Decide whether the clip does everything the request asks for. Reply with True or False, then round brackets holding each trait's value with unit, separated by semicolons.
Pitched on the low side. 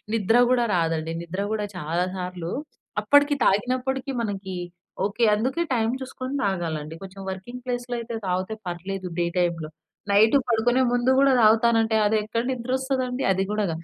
False (220 Hz)